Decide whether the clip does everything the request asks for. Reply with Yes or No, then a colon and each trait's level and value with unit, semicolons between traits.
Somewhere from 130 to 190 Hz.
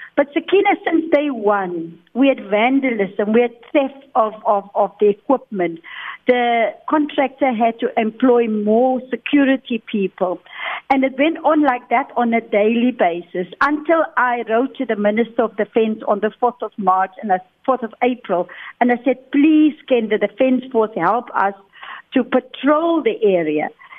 No: high, 240 Hz